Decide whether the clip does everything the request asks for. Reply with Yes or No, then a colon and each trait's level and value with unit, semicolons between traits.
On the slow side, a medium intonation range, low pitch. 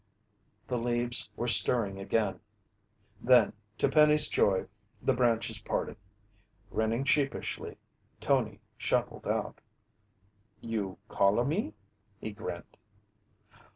Yes: slow, 100 wpm; average, 3.3 semitones; low, 115 Hz